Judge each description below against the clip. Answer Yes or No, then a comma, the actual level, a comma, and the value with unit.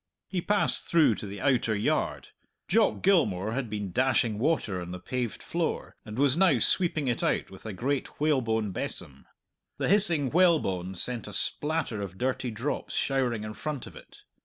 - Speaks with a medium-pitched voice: No, low, 125 Hz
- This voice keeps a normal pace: Yes, average, 175 wpm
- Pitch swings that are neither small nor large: No, wide, 6.3 semitones